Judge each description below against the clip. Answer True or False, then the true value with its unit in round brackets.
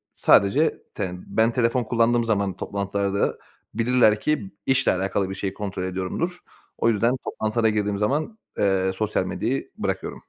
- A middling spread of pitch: True (3.4 semitones)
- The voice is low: True (105 Hz)